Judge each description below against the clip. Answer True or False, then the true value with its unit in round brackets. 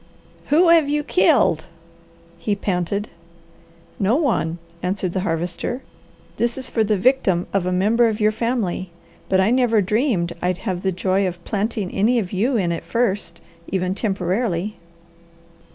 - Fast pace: False (150 wpm)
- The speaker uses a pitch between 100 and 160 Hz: False (200 Hz)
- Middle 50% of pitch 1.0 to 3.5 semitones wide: False (4.2 semitones)